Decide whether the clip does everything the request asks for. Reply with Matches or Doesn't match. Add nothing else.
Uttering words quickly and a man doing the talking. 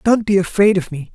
Matches